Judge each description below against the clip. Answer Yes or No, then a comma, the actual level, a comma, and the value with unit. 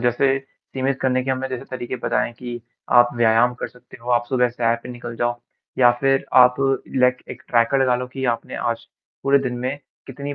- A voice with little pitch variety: Yes, narrow, 1.6 semitones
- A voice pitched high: No, low, 125 Hz